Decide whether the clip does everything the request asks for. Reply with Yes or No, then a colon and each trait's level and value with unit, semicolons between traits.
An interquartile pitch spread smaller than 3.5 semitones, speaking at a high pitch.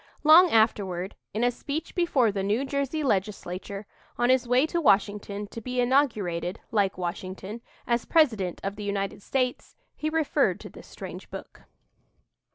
No: average, 5.3 semitones; high, 225 Hz